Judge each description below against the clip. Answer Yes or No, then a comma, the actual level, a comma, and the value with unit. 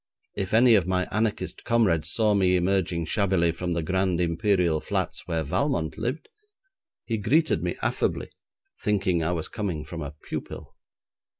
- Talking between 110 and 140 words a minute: No, average, 155 wpm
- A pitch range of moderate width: Yes, average, 4.1 semitones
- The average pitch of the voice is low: Yes, very low, 95 Hz